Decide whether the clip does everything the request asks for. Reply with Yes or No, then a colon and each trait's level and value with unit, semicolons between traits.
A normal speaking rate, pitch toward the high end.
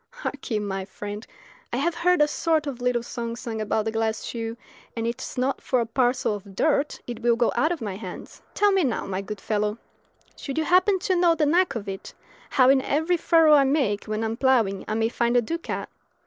No: fast, 230 wpm; high, 240 Hz